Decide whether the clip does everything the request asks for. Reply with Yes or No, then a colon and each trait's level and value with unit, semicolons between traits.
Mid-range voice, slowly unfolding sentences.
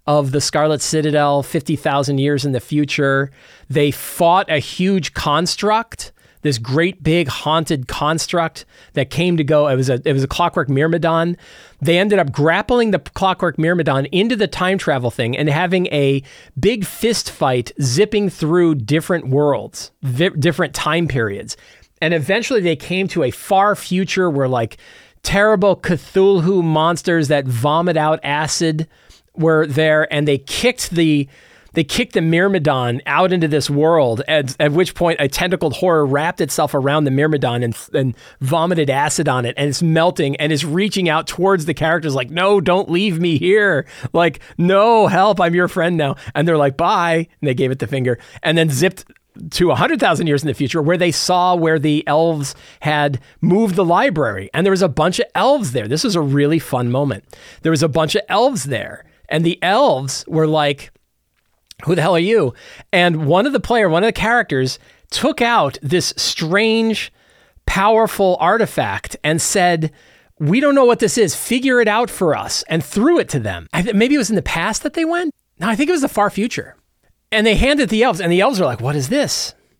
No: medium, 165 Hz; average, 195 wpm